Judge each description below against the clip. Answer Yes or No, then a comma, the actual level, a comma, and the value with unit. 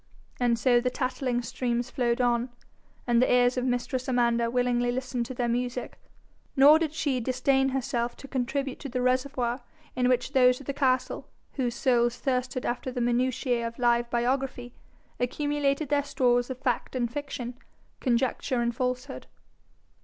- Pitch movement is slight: Yes, narrow, 1.6 semitones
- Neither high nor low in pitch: No, very high, 250 Hz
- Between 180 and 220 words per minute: No, average, 160 wpm